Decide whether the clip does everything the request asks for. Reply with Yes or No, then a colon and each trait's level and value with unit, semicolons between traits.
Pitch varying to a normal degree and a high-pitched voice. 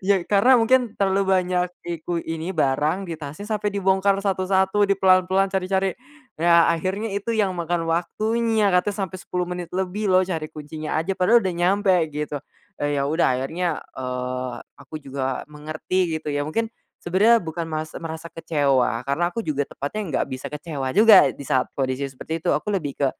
No: average, 4.2 semitones; medium, 175 Hz